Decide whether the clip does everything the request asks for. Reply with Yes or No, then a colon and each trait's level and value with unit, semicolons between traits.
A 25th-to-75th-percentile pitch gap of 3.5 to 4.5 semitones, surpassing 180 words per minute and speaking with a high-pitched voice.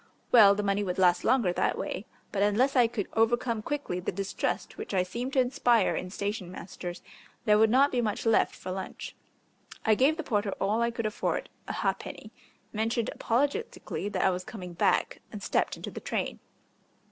Yes: average, 3.8 semitones; average, 190 wpm; high, 215 Hz